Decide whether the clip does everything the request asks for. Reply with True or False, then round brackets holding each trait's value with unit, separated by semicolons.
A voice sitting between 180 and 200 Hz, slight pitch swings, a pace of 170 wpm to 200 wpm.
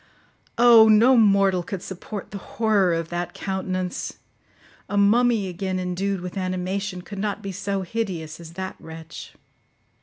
False (190 Hz; 2.3 semitones; 145 wpm)